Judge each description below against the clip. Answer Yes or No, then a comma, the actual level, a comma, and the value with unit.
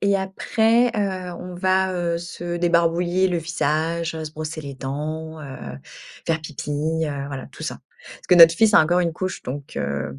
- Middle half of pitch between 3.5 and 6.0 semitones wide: No, average, 2.9 semitones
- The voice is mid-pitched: Yes, medium, 170 Hz